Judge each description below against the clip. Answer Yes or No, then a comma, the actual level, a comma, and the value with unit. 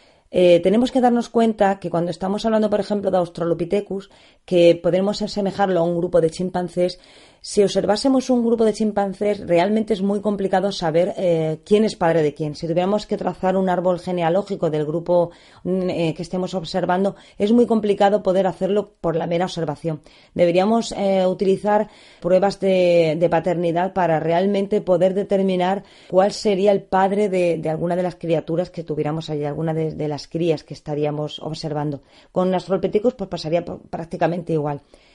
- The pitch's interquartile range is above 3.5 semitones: No, average, 3.1 semitones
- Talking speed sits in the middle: Yes, average, 170 wpm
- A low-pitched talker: No, medium, 185 Hz